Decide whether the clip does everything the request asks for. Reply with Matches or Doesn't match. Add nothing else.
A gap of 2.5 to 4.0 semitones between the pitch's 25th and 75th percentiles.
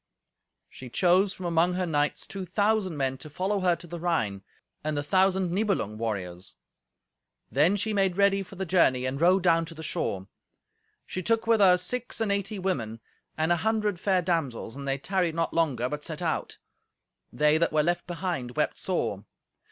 Doesn't match